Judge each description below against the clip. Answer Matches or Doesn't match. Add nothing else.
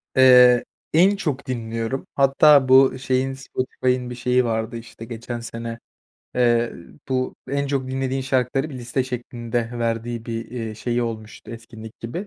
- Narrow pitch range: Matches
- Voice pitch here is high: Doesn't match